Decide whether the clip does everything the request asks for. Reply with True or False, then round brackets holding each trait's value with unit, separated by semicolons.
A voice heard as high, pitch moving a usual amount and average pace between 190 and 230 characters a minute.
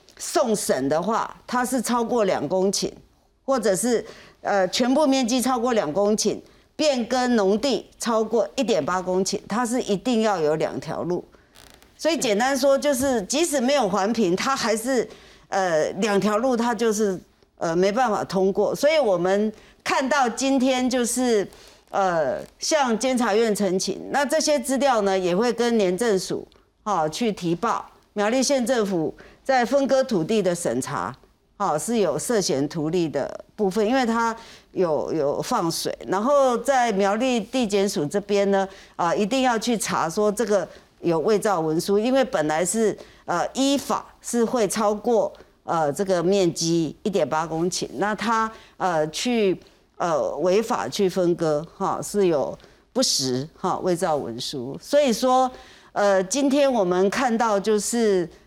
True (210 Hz; 4.7 semitones; 225 characters per minute)